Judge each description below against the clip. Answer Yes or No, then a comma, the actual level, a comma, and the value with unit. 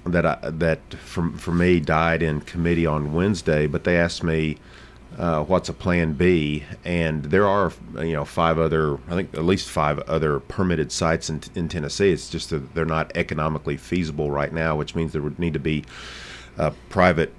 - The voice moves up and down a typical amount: No, narrow, 1.9 semitones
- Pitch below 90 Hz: Yes, very low, 80 Hz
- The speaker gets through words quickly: No, average, 190 wpm